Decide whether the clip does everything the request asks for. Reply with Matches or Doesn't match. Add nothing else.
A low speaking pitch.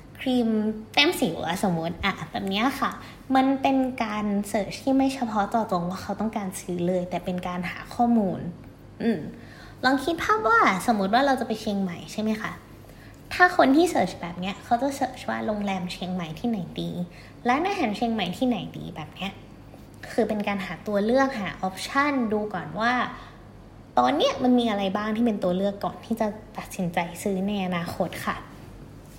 Doesn't match